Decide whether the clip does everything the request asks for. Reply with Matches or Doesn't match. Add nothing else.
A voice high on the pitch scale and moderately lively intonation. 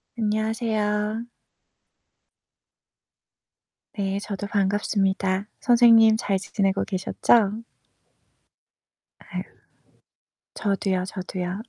Doesn't match